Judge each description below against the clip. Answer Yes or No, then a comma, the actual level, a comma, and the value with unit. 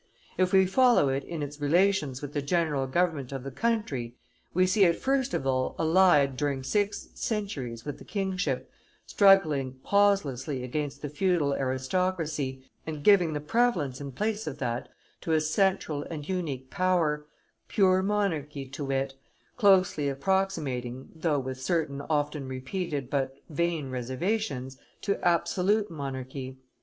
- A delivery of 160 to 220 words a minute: No, average, 145 wpm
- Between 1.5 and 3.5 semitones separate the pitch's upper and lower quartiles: No, wide, 5.6 semitones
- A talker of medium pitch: Yes, medium, 150 Hz